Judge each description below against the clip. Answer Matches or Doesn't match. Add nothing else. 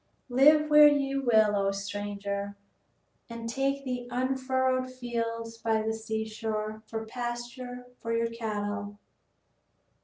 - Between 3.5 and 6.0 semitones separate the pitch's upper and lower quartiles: Doesn't match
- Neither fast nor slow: Doesn't match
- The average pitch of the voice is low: Doesn't match